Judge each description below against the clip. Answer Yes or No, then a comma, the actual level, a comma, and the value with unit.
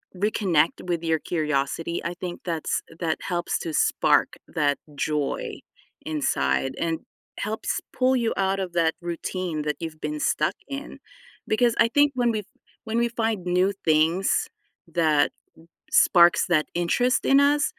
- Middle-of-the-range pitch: Yes, medium, 175 Hz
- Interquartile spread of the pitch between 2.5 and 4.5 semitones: No, wide, 5.6 semitones